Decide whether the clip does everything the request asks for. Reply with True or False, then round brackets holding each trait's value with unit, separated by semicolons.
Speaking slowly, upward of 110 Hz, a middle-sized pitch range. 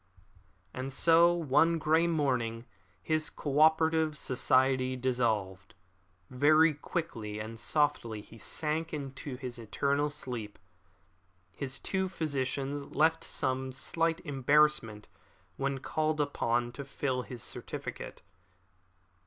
True (110 wpm; 140 Hz; 3.8 semitones)